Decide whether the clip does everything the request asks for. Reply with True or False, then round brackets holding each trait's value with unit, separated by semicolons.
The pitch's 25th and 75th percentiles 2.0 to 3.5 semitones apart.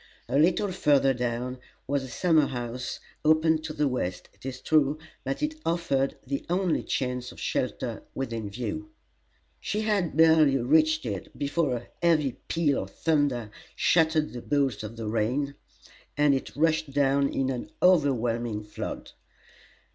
False (4.2 semitones)